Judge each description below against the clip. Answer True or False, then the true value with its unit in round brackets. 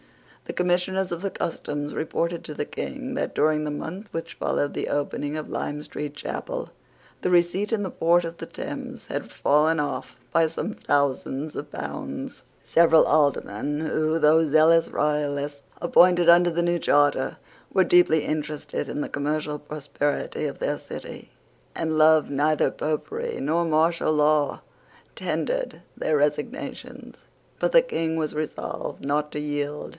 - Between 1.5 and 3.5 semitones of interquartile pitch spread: True (2.7 semitones)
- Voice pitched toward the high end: False (155 Hz)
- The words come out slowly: False (150 wpm)